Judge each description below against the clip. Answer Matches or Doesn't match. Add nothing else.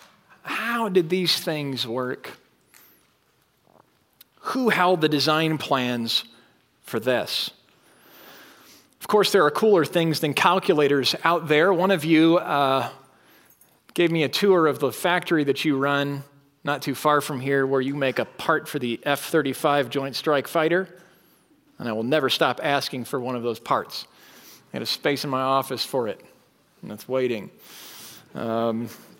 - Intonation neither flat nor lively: Matches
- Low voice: Doesn't match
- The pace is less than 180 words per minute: Matches